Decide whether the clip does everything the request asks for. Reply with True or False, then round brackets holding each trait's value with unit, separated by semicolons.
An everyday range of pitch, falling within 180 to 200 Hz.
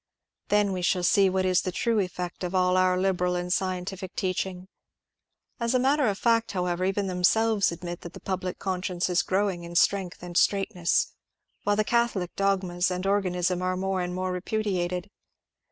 False (1.8 semitones; 185 Hz)